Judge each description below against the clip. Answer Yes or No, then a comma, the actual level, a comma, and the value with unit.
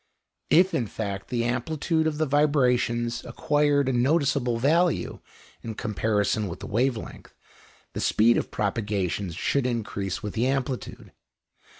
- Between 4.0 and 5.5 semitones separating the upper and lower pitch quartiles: Yes, average, 4.9 semitones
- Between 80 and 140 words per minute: Yes, slow, 135 wpm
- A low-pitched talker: Yes, low, 120 Hz